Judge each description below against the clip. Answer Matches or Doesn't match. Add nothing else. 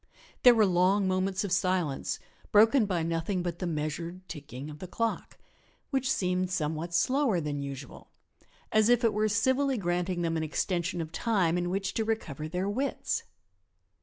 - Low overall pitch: Doesn't match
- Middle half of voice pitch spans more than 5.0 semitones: Doesn't match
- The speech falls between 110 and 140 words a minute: Doesn't match